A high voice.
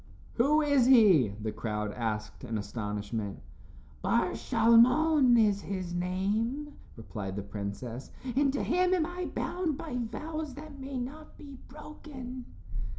Yes: high, 240 Hz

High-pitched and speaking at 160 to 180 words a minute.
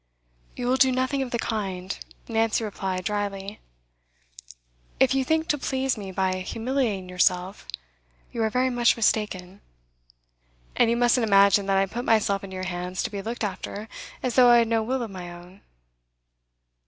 Yes: high, 215 Hz; average, 170 wpm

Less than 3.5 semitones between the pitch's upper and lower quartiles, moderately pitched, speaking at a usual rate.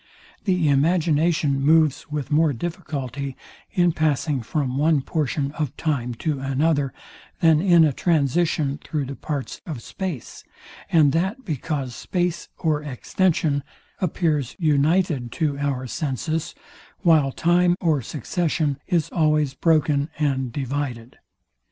No: average, 3.0 semitones; medium, 150 Hz; slow, 120 wpm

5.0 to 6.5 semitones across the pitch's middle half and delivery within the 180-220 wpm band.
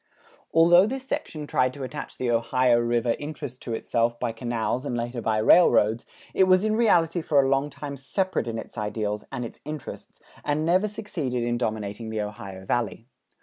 Yes: wide, 5.4 semitones; average, 185 wpm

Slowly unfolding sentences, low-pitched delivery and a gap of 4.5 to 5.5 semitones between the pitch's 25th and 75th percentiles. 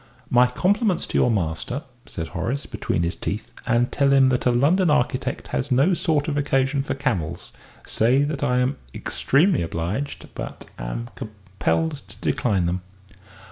No: average, 160 wpm; low, 125 Hz; average, 5.1 semitones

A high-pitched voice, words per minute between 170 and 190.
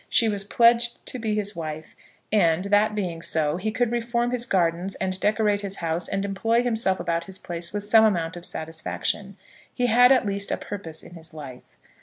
No: high, 200 Hz; average, 200 wpm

